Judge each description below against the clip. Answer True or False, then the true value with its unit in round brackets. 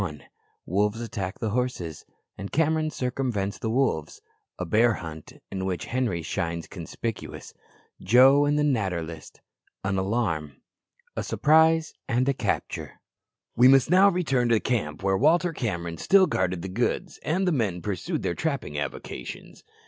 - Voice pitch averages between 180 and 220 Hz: False (115 Hz)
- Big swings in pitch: True (7.1 semitones)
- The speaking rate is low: False (150 wpm)